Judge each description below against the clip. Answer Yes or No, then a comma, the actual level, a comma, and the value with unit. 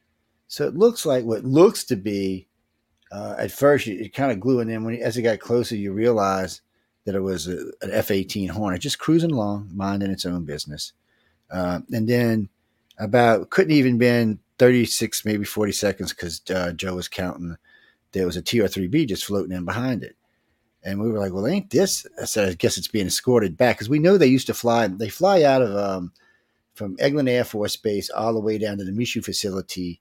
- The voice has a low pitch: Yes, low, 105 Hz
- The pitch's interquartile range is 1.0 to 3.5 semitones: No, average, 4.2 semitones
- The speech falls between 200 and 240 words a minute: Yes, fast, 205 wpm